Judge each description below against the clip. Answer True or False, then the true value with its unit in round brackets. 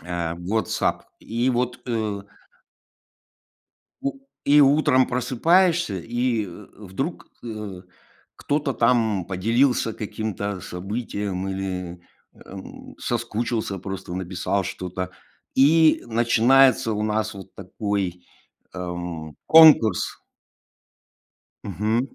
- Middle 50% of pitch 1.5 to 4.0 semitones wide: False (4.7 semitones)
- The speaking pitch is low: True (110 Hz)